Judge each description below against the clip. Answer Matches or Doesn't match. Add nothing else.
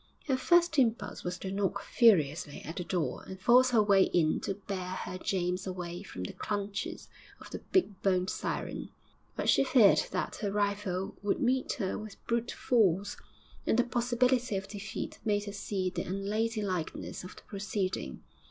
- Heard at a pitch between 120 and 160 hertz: Doesn't match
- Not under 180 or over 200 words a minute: Doesn't match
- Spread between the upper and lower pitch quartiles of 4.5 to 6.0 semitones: Doesn't match